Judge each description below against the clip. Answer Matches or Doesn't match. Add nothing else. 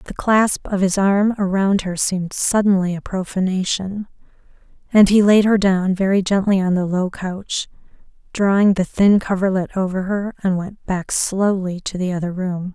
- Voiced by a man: Doesn't match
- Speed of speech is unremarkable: Matches